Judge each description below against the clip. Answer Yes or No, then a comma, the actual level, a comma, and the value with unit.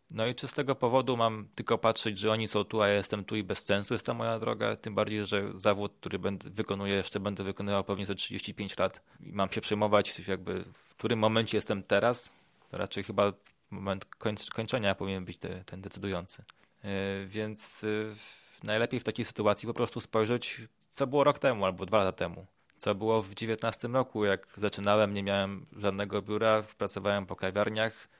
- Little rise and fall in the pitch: Yes, narrow, 2.1 semitones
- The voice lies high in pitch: No, low, 105 Hz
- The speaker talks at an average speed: No, fast, 190 wpm